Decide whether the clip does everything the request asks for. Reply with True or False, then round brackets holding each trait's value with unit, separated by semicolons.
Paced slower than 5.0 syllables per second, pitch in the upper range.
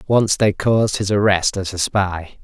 False (4.4 syllables/s; 100 Hz)